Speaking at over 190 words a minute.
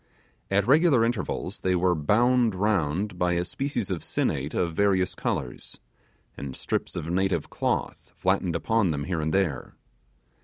No: average, 150 wpm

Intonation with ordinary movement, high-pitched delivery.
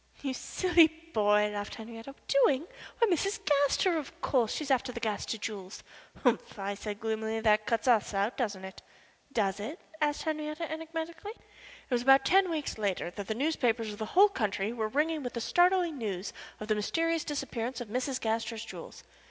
No: wide, 6.4 semitones; high, 245 Hz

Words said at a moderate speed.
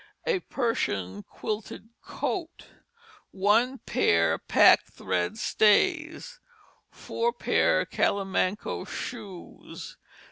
No: slow, 75 wpm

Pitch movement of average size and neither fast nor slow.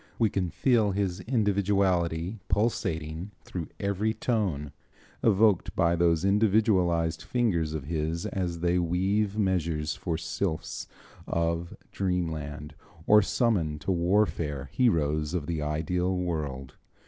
No: average, 3.9 semitones; slow, 115 wpm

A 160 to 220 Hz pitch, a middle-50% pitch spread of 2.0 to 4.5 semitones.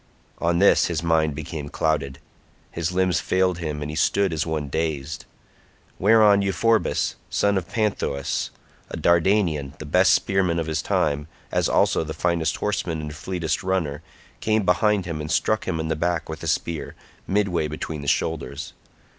No: very low, 80 Hz; average, 3.4 semitones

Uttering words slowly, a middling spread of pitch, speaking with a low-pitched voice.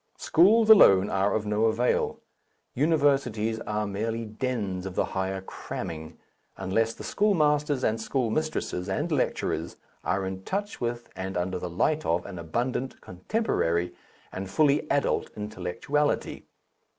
No: slow, 130 wpm; wide, 6.9 semitones; low, 110 Hz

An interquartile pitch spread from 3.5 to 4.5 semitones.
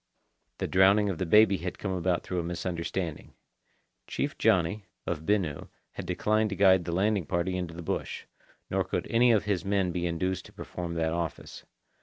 No: average, 2.7 semitones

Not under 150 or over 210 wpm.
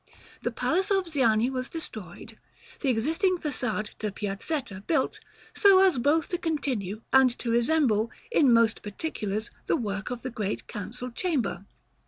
Yes: average, 155 wpm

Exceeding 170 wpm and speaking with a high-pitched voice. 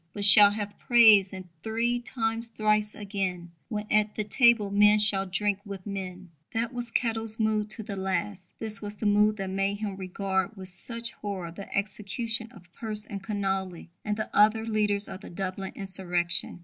Yes: average, 180 wpm; high, 205 Hz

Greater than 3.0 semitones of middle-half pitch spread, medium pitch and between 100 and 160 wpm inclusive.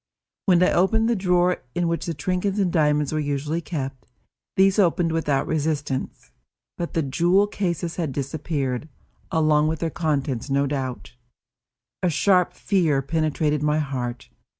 Yes: average, 3.7 semitones; medium, 155 Hz; average, 150 wpm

